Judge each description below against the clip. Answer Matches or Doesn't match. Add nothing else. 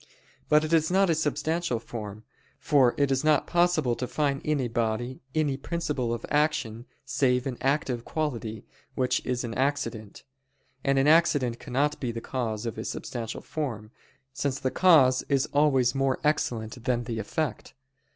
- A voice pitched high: Doesn't match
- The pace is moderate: Matches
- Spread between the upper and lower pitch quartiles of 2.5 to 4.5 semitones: Matches